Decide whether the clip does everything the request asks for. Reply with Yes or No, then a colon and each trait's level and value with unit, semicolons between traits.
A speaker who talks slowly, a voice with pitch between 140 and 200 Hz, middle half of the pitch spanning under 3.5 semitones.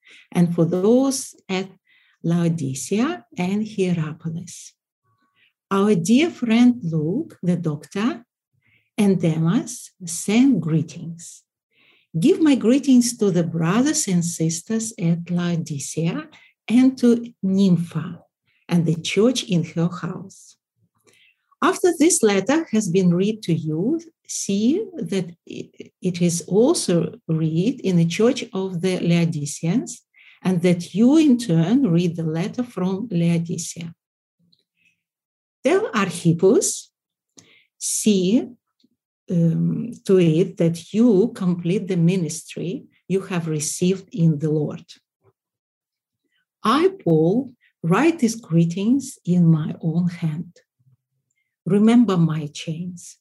No: slow, 105 wpm; medium, 185 Hz; wide, 5.6 semitones